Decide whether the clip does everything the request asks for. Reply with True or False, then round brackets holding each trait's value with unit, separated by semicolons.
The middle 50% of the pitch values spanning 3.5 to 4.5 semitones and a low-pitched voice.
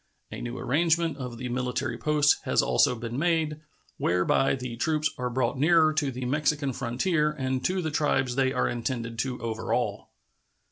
True (3.8 semitones; 130 Hz)